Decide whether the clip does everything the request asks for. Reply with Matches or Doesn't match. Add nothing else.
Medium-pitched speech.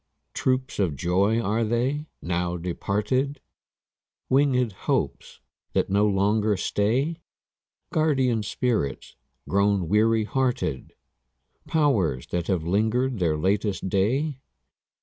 Doesn't match